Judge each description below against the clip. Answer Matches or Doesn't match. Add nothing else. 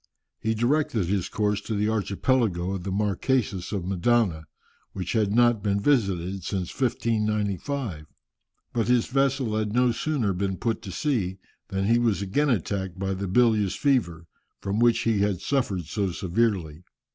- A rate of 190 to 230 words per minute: Doesn't match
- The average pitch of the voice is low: Matches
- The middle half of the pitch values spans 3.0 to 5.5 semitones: Matches